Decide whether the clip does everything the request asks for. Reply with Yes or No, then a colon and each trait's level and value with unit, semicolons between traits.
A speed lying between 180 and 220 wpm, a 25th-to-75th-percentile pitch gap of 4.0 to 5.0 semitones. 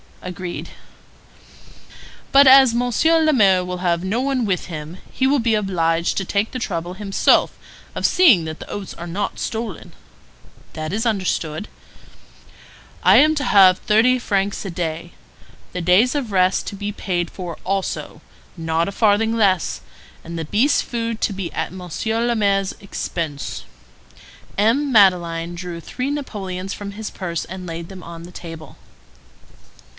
No: average, 155 wpm; average, 4.5 semitones